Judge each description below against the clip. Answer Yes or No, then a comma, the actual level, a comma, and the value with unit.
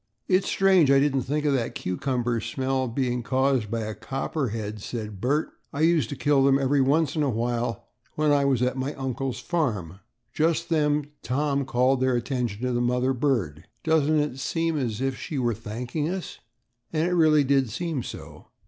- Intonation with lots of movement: No, average, 3.5 semitones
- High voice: No, low, 135 Hz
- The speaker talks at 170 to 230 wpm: Yes, average, 190 wpm